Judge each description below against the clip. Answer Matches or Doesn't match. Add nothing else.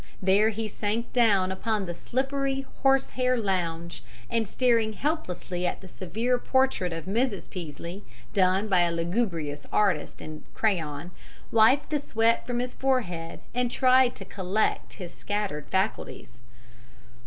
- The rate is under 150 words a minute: Matches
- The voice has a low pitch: Doesn't match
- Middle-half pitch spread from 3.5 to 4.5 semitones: Doesn't match